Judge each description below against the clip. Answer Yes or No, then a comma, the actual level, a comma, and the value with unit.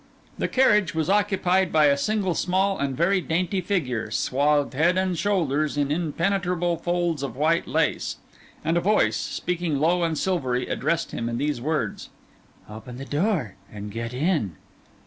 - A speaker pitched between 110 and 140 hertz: No, medium, 165 Hz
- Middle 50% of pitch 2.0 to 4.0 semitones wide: No, average, 4.7 semitones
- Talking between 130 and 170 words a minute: Yes, average, 160 wpm